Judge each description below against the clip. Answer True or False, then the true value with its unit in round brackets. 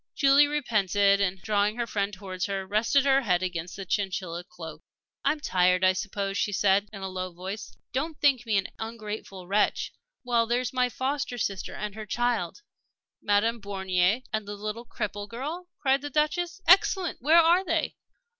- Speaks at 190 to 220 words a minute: False (175 wpm)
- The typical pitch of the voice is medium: False (210 Hz)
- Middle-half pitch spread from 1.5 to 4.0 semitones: False (5.3 semitones)